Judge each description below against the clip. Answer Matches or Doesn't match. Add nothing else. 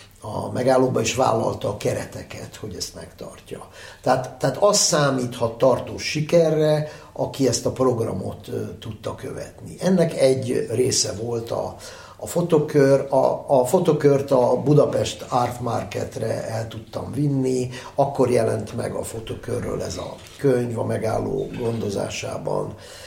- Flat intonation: Doesn't match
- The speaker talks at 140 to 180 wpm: Doesn't match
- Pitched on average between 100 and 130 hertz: Matches